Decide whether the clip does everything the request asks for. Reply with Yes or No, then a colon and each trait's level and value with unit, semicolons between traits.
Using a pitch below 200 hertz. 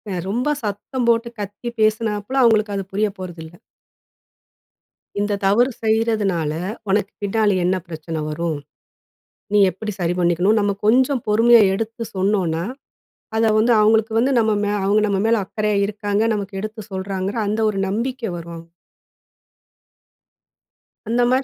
No: high, 210 Hz